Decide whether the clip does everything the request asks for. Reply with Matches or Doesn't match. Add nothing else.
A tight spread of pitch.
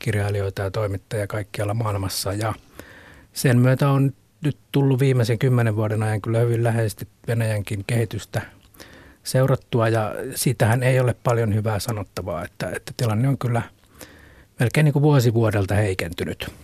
Doesn't match